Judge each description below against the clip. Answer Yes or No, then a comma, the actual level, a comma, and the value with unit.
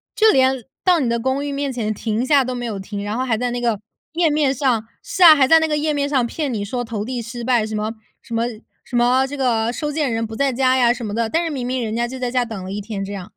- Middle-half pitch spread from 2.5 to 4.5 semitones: Yes, average, 3.5 semitones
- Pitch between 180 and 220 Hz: No, high, 245 Hz